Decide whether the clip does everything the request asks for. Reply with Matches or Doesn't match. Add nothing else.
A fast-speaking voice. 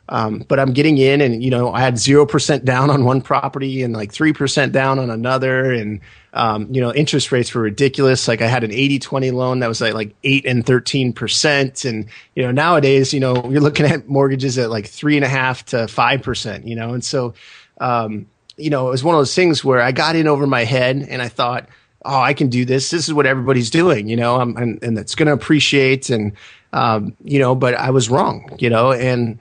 Matches